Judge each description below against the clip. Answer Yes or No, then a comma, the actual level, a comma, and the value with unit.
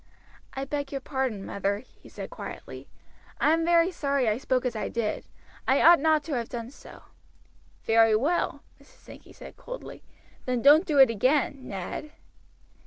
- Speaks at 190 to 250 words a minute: No, average, 170 wpm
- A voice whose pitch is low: No, very high, 265 Hz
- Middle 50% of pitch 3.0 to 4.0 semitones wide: No, average, 4.8 semitones